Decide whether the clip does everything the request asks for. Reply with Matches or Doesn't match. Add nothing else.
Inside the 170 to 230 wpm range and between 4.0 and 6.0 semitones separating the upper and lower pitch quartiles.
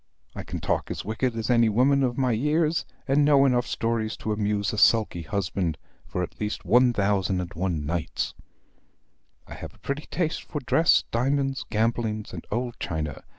Matches